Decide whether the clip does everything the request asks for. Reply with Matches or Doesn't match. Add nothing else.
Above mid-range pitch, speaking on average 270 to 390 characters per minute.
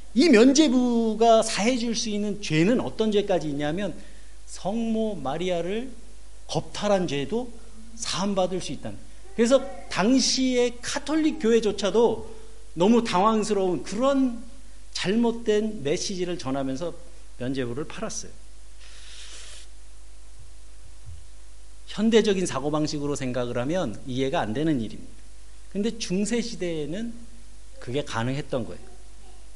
Doesn't match